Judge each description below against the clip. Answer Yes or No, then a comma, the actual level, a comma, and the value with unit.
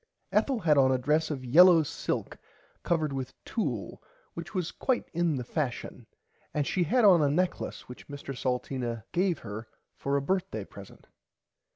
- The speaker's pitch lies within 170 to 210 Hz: No, medium, 150 Hz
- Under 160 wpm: No, average, 165 wpm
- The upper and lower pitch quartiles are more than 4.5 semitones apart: Yes, average, 5.1 semitones